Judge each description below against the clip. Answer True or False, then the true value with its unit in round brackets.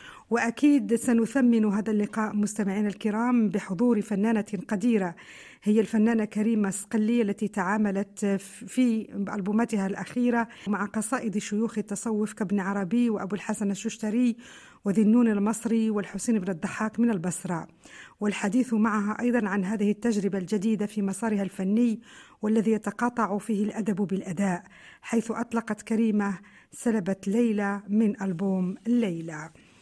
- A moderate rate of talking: True (115 wpm)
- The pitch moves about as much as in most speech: False (2.1 semitones)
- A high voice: True (215 Hz)